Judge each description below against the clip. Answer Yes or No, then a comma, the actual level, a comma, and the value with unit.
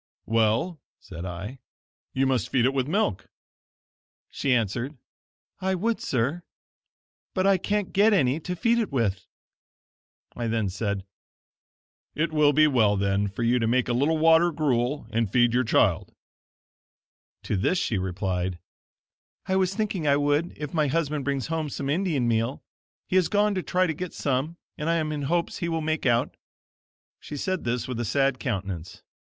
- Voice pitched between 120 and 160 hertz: Yes, medium, 140 Hz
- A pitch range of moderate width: No, wide, 6.3 semitones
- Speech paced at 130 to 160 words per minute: No, average, 170 wpm